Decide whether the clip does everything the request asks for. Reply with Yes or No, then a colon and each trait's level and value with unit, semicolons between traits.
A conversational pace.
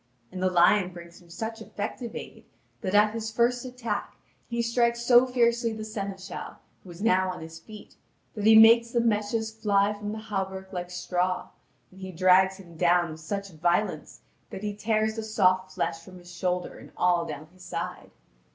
Yes: average, 190 wpm